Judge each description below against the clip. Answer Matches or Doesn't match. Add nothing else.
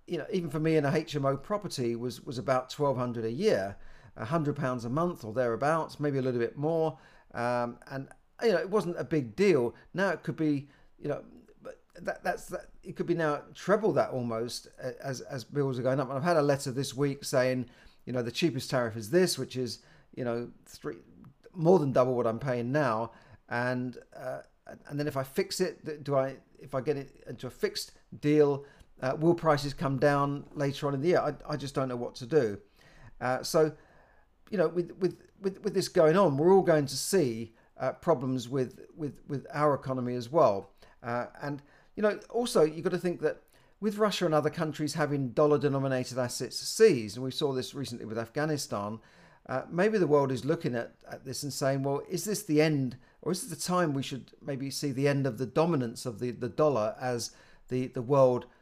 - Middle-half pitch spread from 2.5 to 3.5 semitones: Doesn't match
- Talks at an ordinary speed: Doesn't match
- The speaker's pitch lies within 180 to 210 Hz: Doesn't match